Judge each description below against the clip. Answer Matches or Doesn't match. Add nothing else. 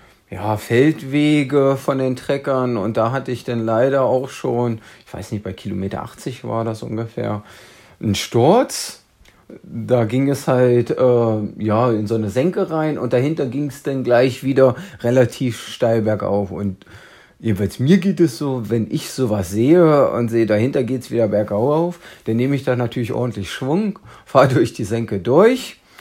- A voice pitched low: Matches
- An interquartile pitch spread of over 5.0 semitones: Doesn't match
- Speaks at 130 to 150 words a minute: Doesn't match